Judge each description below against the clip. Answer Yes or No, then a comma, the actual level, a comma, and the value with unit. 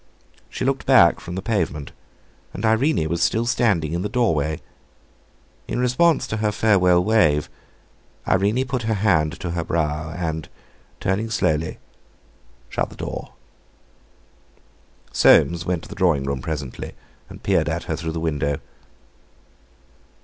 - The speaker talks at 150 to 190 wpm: No, average, 140 wpm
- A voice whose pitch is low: Yes, very low, 90 Hz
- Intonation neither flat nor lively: No, wide, 5.9 semitones